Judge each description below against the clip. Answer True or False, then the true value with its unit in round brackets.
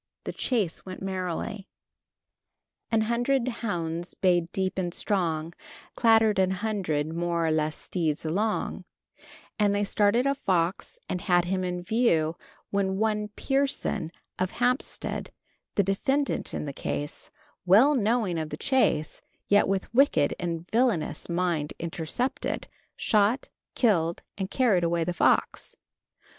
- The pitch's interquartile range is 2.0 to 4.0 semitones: False (4.6 semitones)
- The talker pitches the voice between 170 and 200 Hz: True (190 Hz)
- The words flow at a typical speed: False (130 wpm)